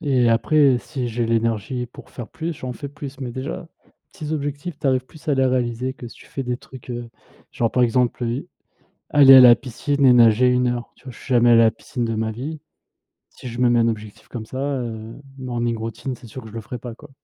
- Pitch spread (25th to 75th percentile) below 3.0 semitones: Yes, narrow, 2.5 semitones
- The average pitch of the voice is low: Yes, low, 125 Hz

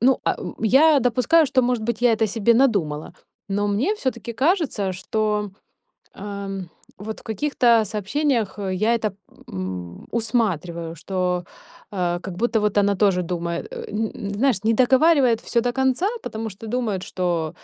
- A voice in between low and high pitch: No, high, 215 Hz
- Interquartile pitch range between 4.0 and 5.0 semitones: Yes, average, 4.3 semitones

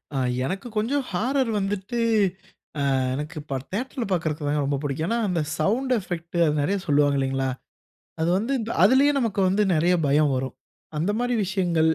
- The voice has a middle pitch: Yes, medium, 180 Hz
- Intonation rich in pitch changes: Yes, wide, 7.2 semitones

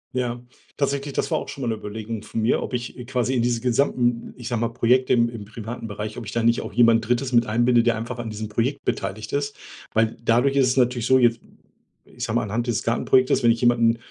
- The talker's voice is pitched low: Yes, low, 120 Hz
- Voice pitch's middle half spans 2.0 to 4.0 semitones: No, narrow, 1.6 semitones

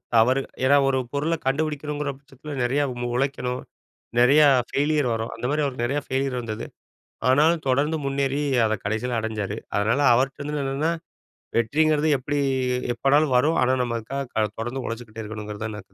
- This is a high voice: No, low, 135 Hz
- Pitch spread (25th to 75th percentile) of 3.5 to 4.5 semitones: Yes, average, 3.9 semitones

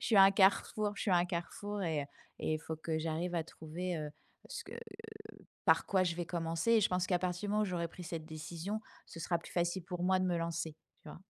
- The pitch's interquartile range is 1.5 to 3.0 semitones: Yes, average, 2.7 semitones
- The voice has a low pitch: No, medium, 175 Hz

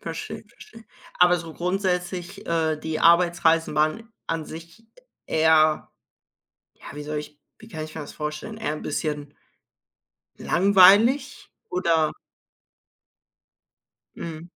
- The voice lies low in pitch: No, medium, 165 Hz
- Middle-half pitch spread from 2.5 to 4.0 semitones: Yes, average, 2.8 semitones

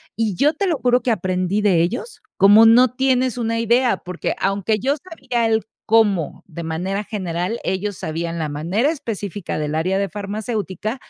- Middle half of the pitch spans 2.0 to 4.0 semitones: No, average, 4.6 semitones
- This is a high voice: Yes, high, 210 Hz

